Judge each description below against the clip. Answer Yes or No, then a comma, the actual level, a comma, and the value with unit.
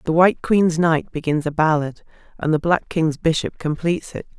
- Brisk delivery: No, average, 190 wpm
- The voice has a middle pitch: Yes, medium, 160 Hz